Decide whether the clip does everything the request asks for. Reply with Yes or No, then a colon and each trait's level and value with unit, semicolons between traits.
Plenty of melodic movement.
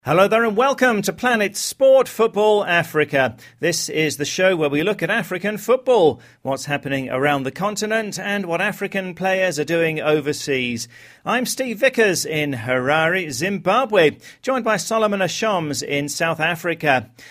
Yes: wide, 6.2 semitones